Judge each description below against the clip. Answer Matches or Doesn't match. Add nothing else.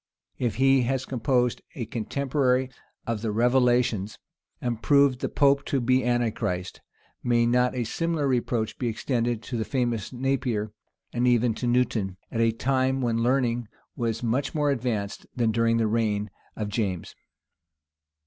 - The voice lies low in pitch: Matches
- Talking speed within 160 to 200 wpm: Doesn't match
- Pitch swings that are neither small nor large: Doesn't match